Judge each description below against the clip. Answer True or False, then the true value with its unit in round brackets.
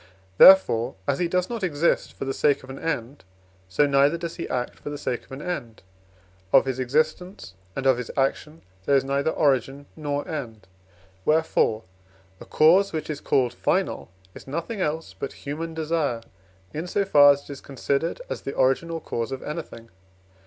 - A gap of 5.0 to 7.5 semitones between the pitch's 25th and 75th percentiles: False (3.5 semitones)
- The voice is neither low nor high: True (145 Hz)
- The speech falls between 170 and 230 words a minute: True (185 wpm)